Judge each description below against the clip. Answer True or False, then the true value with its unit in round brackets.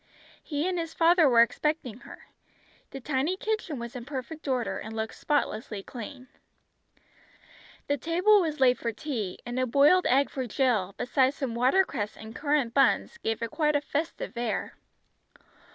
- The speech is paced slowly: False (160 wpm)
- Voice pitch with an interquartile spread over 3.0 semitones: True (4.4 semitones)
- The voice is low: False (270 Hz)